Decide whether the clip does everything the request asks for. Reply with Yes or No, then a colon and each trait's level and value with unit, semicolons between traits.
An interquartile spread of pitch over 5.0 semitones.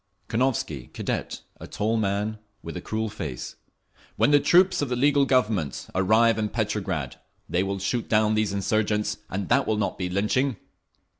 No: average, 3.1 semitones